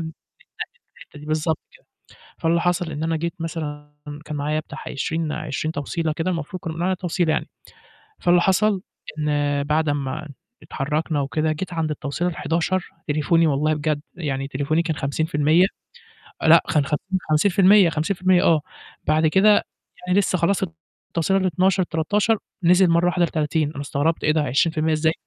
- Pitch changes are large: No, average, 2.7 semitones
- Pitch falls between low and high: Yes, medium, 160 Hz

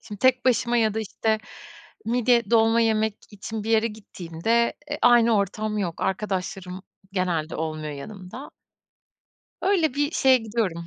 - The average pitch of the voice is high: Yes, high, 220 Hz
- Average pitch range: Yes, average, 3.8 semitones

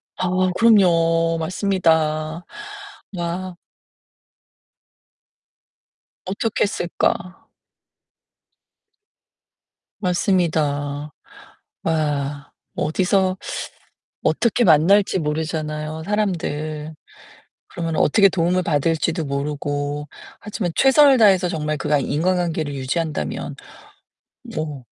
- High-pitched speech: No, medium, 165 Hz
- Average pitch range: Yes, average, 3.5 semitones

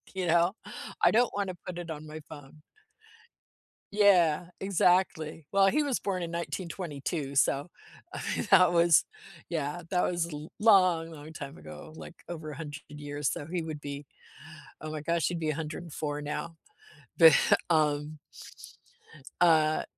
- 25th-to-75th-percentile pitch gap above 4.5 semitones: No, average, 2.9 semitones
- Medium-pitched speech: Yes, medium, 165 Hz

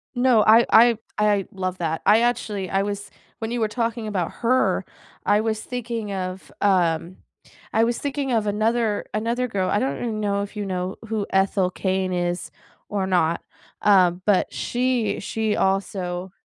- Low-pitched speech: No, high, 205 Hz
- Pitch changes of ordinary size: Yes, average, 3.3 semitones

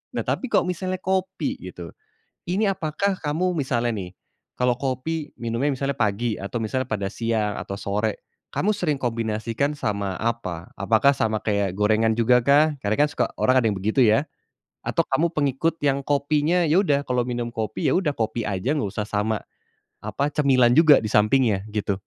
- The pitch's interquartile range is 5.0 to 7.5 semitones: Yes, wide, 5.4 semitones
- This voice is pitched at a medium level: No, low, 120 Hz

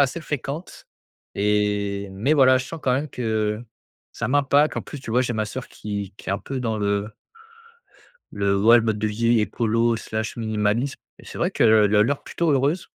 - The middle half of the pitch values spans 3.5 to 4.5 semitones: Yes, average, 4.0 semitones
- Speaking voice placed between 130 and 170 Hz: No, low, 115 Hz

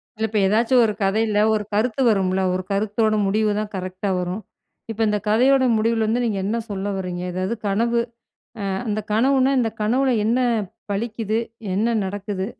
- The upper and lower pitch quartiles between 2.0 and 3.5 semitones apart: Yes, narrow, 2.5 semitones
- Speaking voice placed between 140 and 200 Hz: No, high, 215 Hz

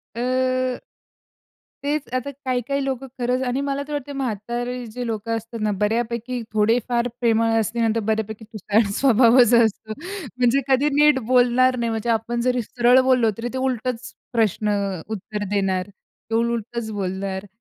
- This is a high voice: Yes, high, 235 Hz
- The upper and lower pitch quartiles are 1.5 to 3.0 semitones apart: Yes, narrow, 2.6 semitones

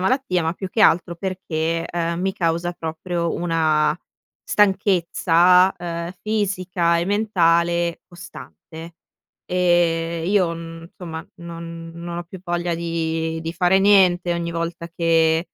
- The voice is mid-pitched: Yes, medium, 170 Hz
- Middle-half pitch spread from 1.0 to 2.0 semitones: Yes, narrow, 1.5 semitones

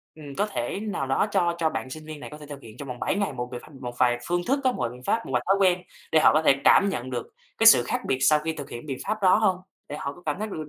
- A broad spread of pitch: Yes, wide, 6.4 semitones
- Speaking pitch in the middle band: Yes, medium, 150 Hz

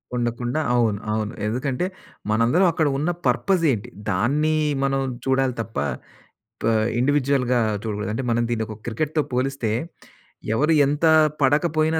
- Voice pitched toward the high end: No, low, 130 Hz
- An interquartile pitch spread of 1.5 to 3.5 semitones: No, average, 4.2 semitones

